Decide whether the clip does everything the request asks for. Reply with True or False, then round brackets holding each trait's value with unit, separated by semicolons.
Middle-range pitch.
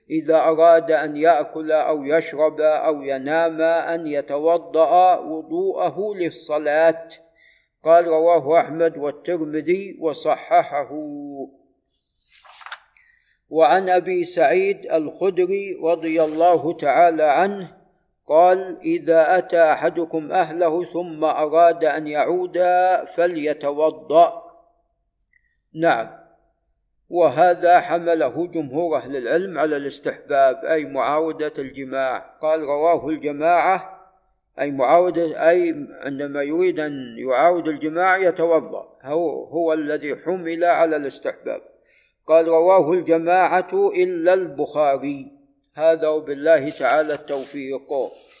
True (165 Hz)